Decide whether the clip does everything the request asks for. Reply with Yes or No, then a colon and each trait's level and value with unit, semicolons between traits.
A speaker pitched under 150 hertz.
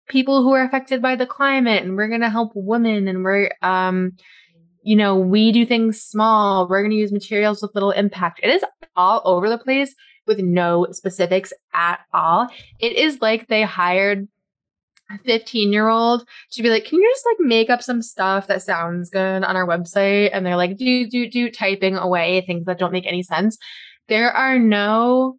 No: high, 210 Hz